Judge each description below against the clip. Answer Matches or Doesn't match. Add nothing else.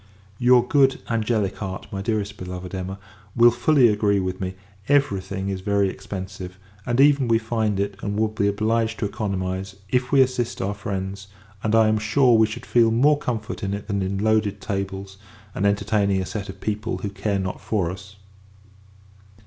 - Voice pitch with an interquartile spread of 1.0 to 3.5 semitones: Matches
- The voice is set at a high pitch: Doesn't match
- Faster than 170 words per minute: Matches